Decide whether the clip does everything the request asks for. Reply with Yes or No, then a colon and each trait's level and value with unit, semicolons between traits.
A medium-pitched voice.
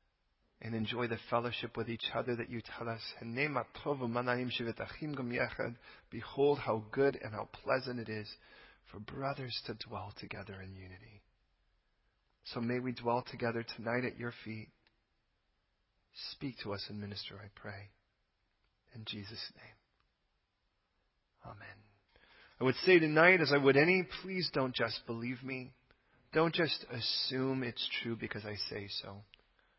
No: low, 120 Hz